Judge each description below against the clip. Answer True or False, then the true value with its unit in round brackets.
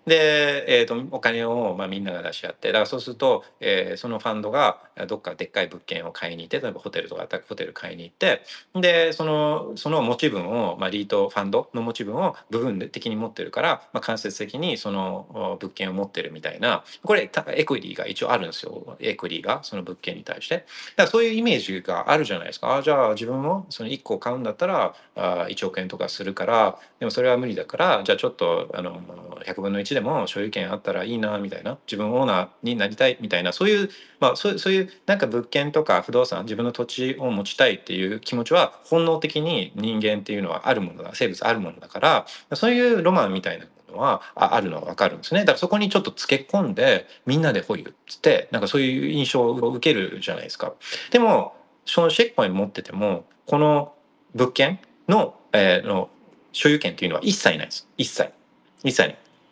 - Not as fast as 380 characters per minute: False (445 characters per minute)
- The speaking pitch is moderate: True (155 Hz)